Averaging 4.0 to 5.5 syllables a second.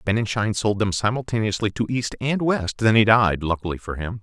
Yes: 5.4 syllables/s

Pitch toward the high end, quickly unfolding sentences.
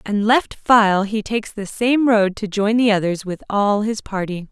Yes: high, 210 Hz; fast, 210 wpm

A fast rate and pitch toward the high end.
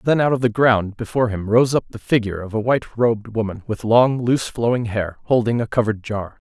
No: fast, 230 wpm; low, 115 Hz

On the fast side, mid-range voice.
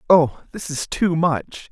No: average, 175 wpm; medium, 155 Hz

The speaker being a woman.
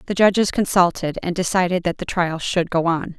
Yes: female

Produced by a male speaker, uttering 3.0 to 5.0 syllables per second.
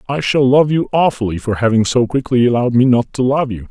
No: male; 6.0 syllables/s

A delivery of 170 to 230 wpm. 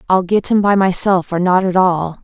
No: fast, 240 wpm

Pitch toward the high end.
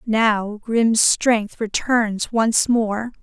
Yes: high, 220 Hz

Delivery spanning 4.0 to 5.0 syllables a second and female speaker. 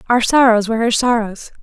No: 5.9 syllables/s; female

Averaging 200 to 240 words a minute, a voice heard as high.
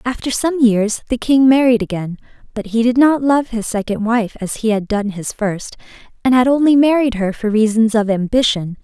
Yes: fast, 205 wpm; high, 230 Hz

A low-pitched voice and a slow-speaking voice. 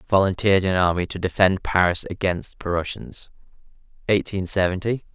Yes: very low, 95 Hz; slow, 115 wpm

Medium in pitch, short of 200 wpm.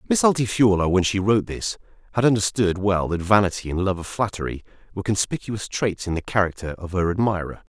No: low, 100 Hz; average, 185 wpm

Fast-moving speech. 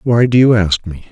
Yes: fast, 270 wpm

